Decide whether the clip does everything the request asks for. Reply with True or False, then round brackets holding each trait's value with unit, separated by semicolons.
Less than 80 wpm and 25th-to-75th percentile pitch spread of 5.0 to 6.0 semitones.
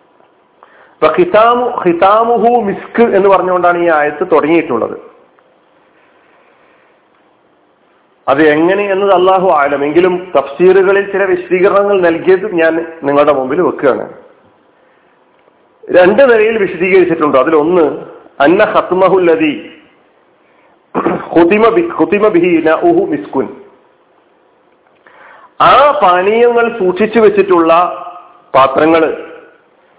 True (65 wpm; 5.4 semitones)